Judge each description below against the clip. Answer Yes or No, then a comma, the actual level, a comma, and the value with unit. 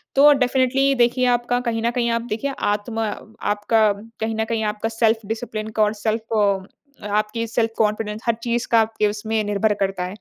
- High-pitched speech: Yes, high, 225 Hz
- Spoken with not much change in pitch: Yes, narrow, 1.9 semitones